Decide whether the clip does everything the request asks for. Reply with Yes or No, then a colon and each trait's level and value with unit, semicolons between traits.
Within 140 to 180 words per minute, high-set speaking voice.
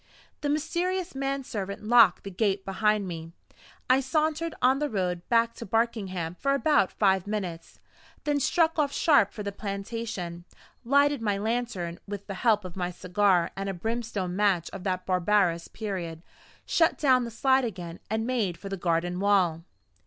Yes: average, 165 wpm; high, 205 Hz